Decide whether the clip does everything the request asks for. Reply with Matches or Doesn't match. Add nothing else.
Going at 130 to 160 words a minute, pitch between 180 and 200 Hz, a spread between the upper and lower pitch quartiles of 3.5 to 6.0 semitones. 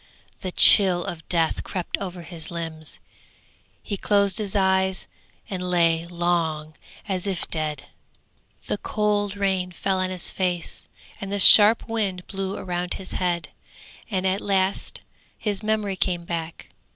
Doesn't match